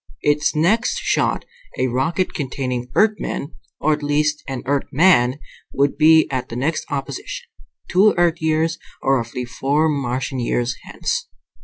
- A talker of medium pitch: Yes, medium, 150 Hz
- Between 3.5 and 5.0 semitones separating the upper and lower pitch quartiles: Yes, average, 4.2 semitones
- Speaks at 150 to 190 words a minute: No, average, 140 wpm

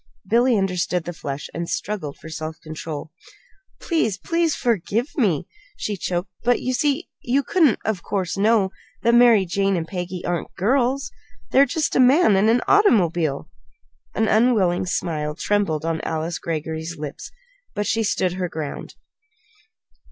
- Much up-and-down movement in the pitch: Yes, wide, 6.4 semitones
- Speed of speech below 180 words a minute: Yes, average, 150 wpm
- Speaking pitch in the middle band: No, high, 195 Hz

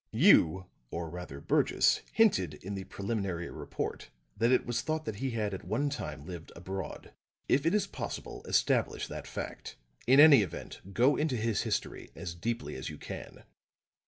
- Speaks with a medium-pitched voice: No, low, 100 Hz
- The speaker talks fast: No, average, 170 wpm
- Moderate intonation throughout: No, wide, 6.9 semitones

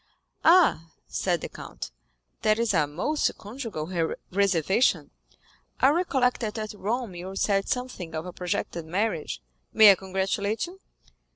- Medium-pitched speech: No, high, 200 Hz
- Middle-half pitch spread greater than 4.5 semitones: Yes, average, 5.1 semitones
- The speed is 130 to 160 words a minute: Yes, slow, 135 wpm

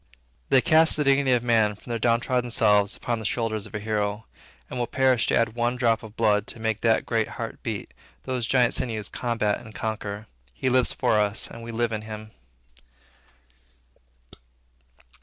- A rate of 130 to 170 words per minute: No, average, 180 wpm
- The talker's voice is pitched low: Yes, low, 115 Hz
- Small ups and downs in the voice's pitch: Yes, narrow, 2.2 semitones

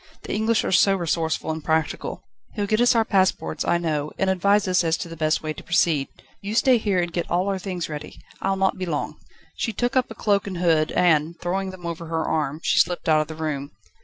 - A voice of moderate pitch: Yes, medium, 175 Hz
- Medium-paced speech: No, fast, 245 wpm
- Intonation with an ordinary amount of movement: Yes, average, 3.5 semitones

